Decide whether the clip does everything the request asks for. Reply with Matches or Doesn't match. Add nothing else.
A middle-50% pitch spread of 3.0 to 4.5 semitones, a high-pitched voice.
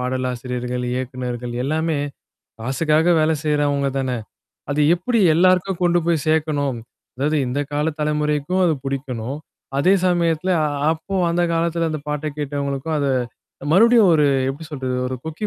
Doesn't match